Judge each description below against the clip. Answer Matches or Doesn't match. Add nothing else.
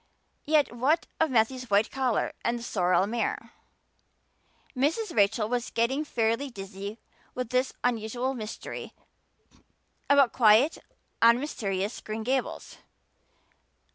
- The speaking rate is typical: Doesn't match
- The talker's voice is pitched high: Matches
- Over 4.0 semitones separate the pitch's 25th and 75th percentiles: Doesn't match